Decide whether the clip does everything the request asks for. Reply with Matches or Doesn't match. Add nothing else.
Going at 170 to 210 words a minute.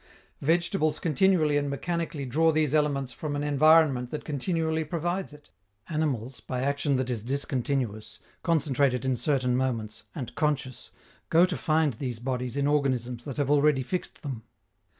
Doesn't match